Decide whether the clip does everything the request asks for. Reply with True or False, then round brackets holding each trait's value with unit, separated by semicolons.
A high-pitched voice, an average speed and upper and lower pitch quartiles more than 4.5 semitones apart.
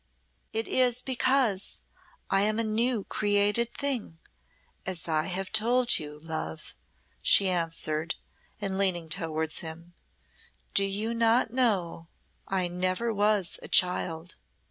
False (195 Hz; 120 wpm; 5.1 semitones)